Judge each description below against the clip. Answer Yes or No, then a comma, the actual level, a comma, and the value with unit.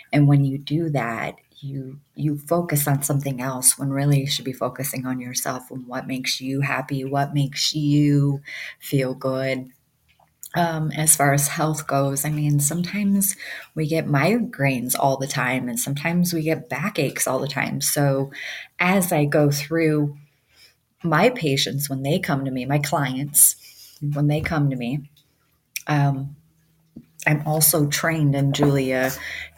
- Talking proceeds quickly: No, average, 155 wpm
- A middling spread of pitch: No, narrow, 2.1 semitones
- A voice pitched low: No, medium, 145 Hz